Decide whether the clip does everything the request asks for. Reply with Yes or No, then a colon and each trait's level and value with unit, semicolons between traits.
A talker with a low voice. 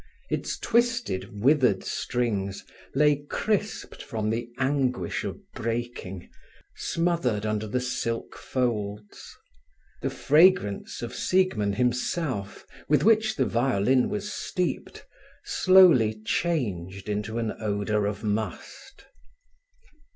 Yes: low, 120 Hz